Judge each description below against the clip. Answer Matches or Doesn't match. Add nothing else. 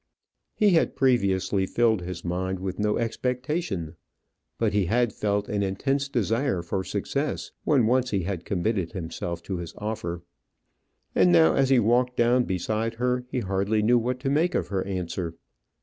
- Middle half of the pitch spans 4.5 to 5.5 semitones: Matches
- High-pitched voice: Doesn't match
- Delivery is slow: Doesn't match